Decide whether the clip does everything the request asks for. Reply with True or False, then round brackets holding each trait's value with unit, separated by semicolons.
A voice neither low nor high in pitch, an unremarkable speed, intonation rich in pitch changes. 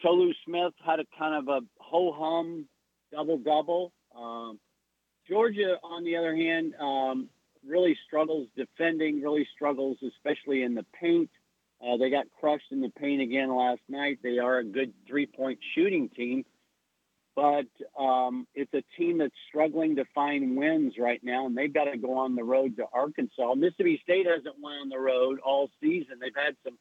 False (145 Hz; 170 wpm; 4.2 semitones)